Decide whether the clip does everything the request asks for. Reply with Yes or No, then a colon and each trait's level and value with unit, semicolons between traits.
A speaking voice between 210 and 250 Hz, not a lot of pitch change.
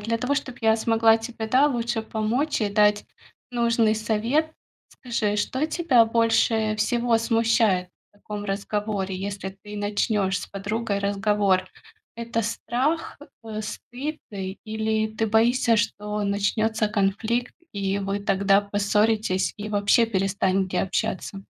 Yes: high, 215 Hz; narrow, 2.2 semitones